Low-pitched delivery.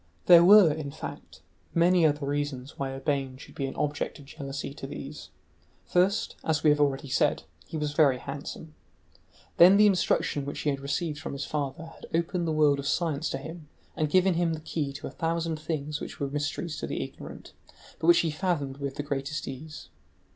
No: medium, 150 Hz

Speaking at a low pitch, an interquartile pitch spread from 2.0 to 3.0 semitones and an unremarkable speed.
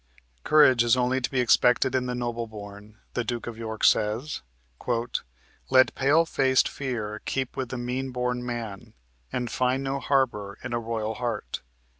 Yes: low, 125 Hz; narrow, 2.4 semitones; average, 165 wpm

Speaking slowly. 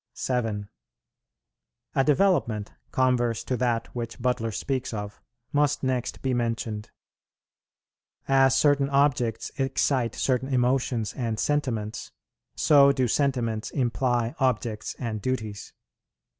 Yes: slow, 105 wpm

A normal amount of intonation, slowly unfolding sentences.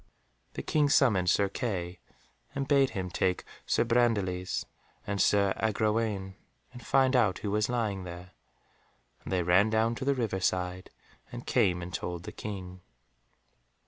No: average, 4.1 semitones; average, 150 wpm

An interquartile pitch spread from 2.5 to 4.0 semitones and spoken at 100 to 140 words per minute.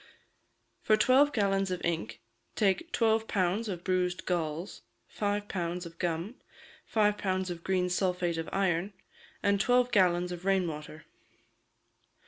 Yes: average, 2.8 semitones; slow, 135 wpm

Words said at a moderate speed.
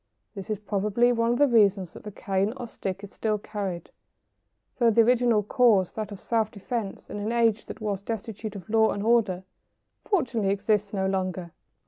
Yes: average, 185 wpm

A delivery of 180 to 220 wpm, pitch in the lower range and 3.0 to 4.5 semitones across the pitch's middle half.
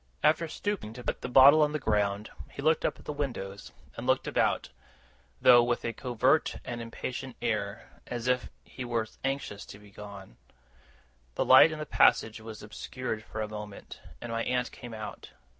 Yes: average, 185 wpm; low, 120 Hz; average, 3.8 semitones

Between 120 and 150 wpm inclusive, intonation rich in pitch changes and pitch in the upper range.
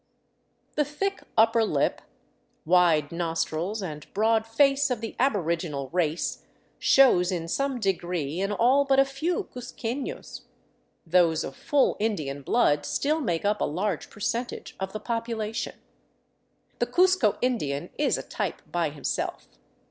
Yes: slow, 135 wpm; wide, 7.0 semitones; high, 210 Hz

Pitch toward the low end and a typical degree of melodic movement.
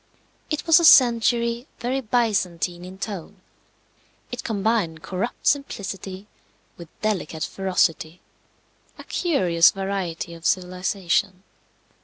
No: high, 195 Hz; average, 4.7 semitones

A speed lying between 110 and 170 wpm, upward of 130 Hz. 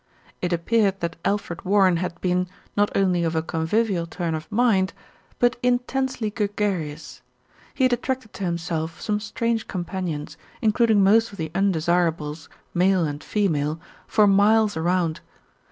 Yes: average, 140 wpm; high, 190 Hz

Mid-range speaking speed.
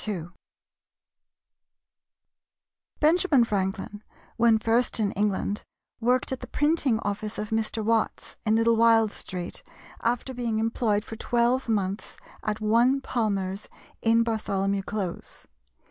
No: slow, 115 wpm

